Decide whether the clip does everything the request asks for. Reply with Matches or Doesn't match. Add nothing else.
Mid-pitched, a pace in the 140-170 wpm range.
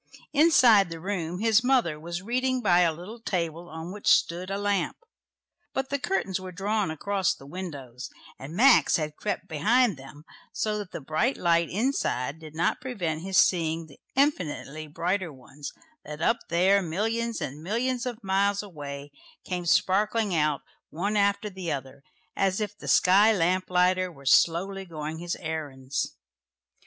Matches